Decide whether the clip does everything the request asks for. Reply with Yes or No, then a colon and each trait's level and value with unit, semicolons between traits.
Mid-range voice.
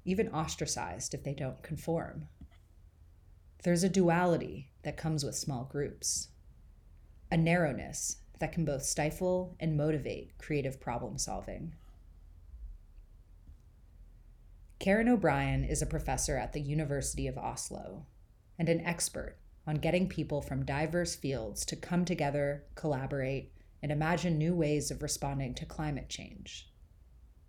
Yes: medium, 145 Hz